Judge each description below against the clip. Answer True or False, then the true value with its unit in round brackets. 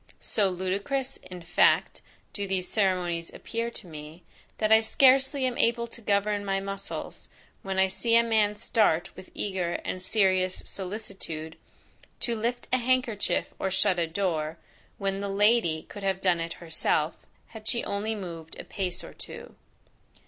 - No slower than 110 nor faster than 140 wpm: False (160 wpm)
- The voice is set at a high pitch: True (195 Hz)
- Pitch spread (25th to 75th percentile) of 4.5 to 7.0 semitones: False (3.6 semitones)